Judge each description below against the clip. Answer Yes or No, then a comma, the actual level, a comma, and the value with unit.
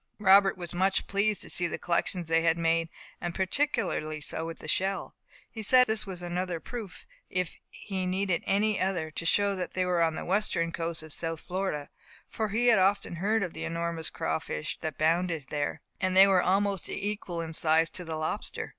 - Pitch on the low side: No, medium, 180 Hz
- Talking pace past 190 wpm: Yes, average, 200 wpm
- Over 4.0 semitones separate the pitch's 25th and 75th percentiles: No, average, 3.0 semitones